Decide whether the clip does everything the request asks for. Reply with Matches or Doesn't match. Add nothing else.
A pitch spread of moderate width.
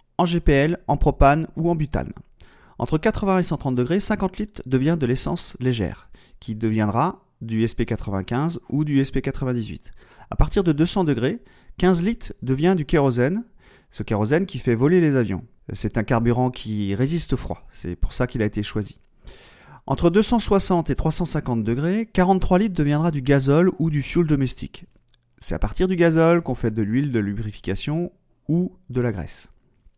Doesn't match